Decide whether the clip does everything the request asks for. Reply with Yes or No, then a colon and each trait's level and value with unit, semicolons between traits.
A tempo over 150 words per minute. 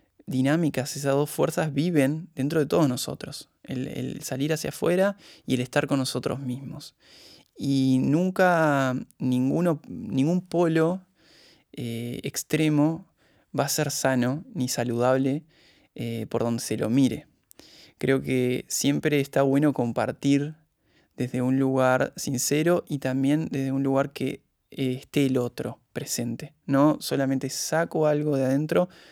No: average, 135 wpm